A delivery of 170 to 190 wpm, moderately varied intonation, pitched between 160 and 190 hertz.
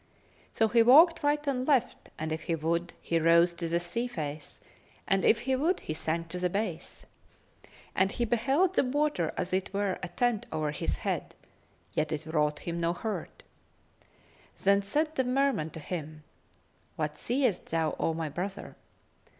No: average, 175 wpm; wide, 7.5 semitones; medium, 185 Hz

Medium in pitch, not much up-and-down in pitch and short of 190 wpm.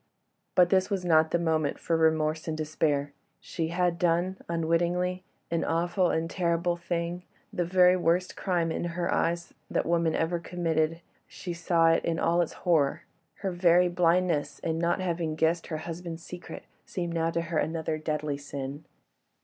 Yes: medium, 170 Hz; narrow, 1.5 semitones; average, 155 wpm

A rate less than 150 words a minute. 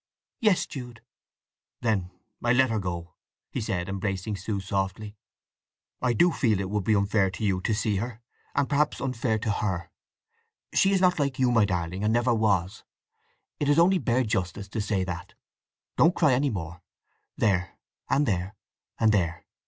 No: average, 175 wpm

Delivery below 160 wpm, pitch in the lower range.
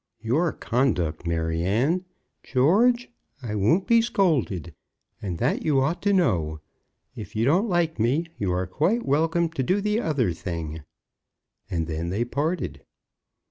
Yes: average, 145 wpm; low, 130 Hz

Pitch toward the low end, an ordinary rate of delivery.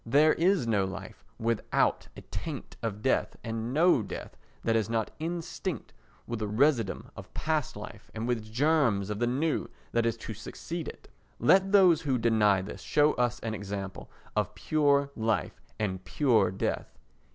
Yes: low, 115 Hz; average, 165 wpm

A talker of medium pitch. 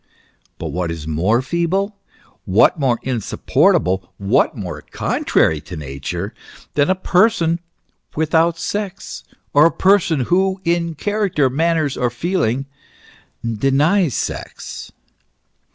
Yes: medium, 150 Hz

